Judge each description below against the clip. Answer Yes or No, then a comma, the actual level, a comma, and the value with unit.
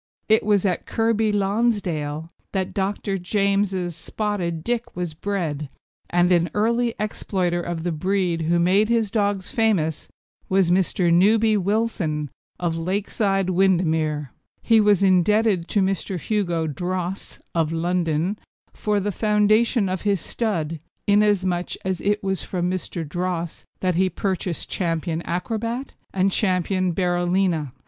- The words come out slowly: Yes, slow, 130 wpm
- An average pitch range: Yes, average, 3.2 semitones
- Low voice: No, medium, 185 Hz